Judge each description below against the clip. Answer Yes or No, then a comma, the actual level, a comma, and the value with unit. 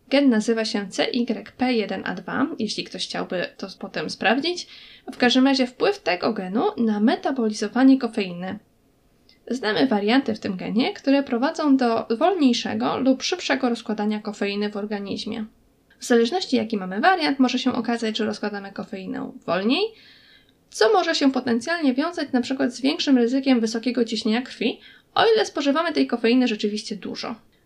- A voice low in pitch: No, high, 240 Hz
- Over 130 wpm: Yes, average, 140 wpm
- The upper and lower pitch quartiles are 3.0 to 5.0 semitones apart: Yes, average, 3.5 semitones